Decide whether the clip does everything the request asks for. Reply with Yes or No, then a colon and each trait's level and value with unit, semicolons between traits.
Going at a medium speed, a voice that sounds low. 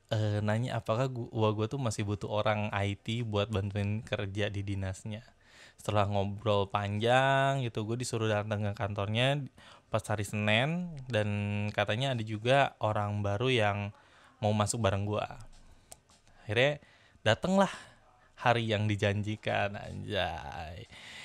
Yes: average, 120 wpm; low, 105 Hz